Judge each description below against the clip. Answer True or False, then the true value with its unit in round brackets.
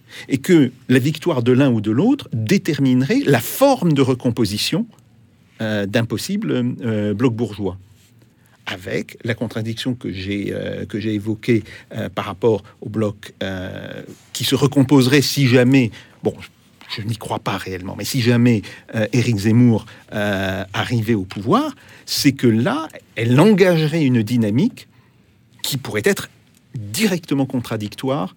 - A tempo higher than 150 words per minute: False (145 wpm)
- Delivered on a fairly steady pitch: False (3.9 semitones)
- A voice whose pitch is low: True (120 Hz)